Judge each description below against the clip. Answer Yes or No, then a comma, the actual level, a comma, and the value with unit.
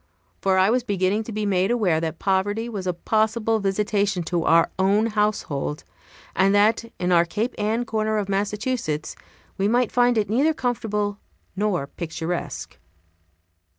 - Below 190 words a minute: Yes, average, 150 wpm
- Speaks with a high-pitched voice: Yes, high, 205 Hz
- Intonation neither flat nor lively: Yes, average, 3.0 semitones